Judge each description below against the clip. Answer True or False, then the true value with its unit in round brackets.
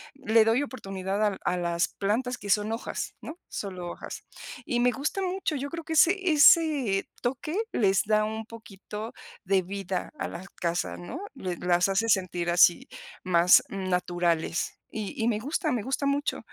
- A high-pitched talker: True (210 Hz)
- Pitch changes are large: True (6.2 semitones)